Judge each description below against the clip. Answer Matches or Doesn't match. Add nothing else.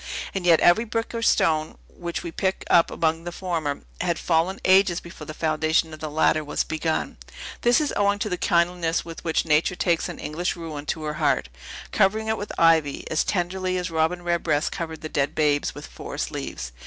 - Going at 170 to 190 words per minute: Doesn't match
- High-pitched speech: Doesn't match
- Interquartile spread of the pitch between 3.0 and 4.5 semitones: Doesn't match